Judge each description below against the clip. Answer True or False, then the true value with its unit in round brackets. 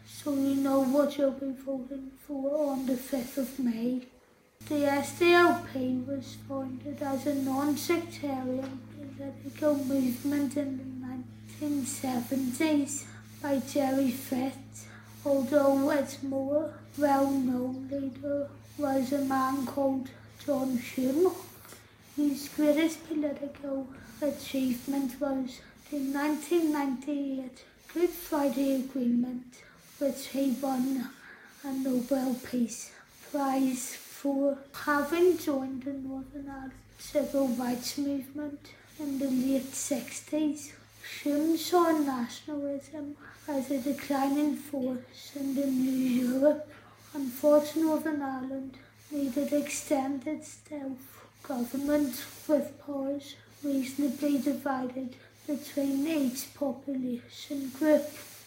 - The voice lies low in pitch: False (275 Hz)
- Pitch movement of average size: False (1.6 semitones)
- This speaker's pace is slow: True (100 wpm)